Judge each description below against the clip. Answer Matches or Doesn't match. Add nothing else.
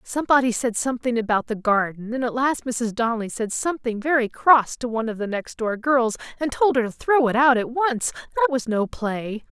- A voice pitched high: Matches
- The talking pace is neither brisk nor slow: Doesn't match